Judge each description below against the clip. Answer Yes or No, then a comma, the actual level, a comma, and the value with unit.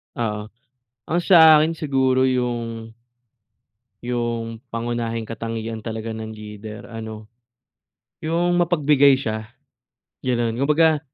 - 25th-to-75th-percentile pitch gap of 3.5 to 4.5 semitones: Yes, average, 4.1 semitones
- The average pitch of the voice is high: No, low, 120 Hz